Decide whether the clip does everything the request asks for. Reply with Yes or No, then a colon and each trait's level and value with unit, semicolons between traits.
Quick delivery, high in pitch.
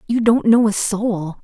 Yes: fast, 210 wpm; high, 215 Hz